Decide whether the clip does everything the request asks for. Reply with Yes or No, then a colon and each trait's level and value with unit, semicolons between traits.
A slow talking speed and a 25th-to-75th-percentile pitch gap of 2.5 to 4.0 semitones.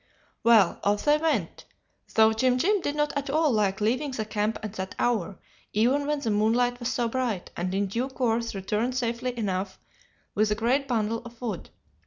No: average, 190 wpm; average, 3.5 semitones